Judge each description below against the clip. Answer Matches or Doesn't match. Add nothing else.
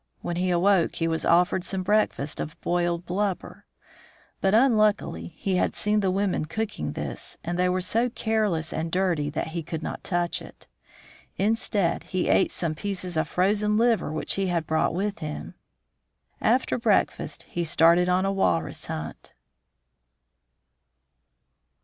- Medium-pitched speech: Matches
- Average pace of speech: Matches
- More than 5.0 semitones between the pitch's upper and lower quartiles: Doesn't match